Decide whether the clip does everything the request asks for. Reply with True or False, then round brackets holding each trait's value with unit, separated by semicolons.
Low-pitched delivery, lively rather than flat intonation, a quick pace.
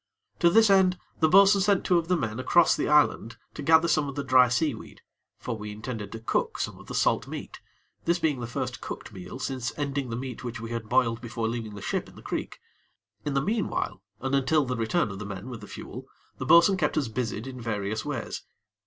True (130 Hz; 5.9 semitones; 230 wpm)